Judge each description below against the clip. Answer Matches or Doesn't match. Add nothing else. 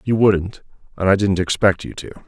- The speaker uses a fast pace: Matches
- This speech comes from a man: Matches